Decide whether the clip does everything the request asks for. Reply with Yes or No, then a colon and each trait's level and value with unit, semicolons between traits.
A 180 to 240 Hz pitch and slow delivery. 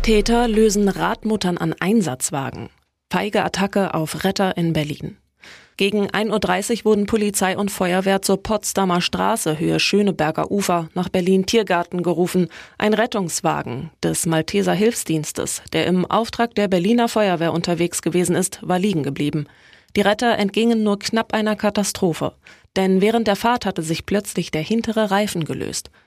No: high, 190 Hz; average, 145 wpm